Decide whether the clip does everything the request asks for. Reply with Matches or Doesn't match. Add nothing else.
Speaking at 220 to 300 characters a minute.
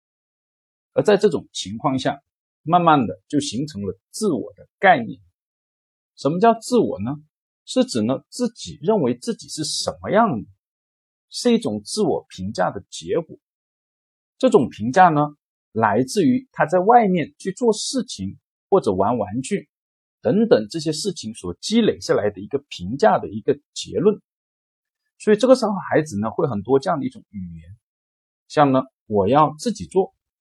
Matches